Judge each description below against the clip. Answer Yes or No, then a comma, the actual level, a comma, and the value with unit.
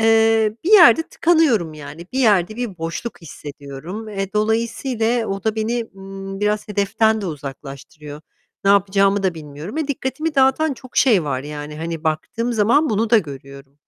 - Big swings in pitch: Yes, wide, 6.4 semitones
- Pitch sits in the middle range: No, high, 205 Hz